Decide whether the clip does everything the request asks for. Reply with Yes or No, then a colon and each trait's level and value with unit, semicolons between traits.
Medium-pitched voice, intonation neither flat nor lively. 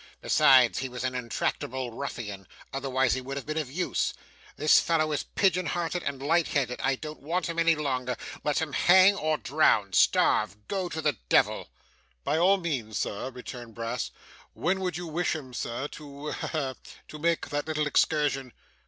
Yes: medium, 145 Hz; average, 4.2 semitones